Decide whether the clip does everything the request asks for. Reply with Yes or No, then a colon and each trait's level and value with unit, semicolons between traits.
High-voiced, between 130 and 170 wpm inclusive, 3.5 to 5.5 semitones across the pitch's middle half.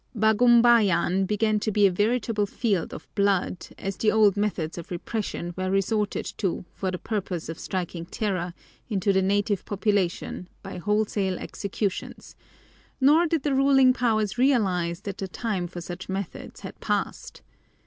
No: high, 200 Hz; average, 150 wpm; average, 3.0 semitones